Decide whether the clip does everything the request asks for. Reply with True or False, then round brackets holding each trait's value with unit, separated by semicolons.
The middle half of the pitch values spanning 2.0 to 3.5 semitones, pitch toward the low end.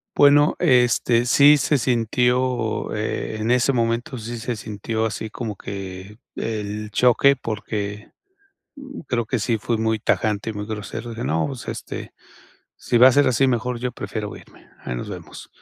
True (2.9 semitones; 115 Hz)